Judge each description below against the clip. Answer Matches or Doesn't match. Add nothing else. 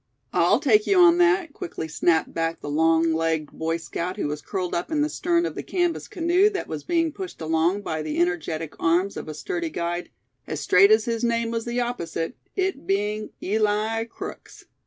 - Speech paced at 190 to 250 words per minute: Matches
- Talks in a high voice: Matches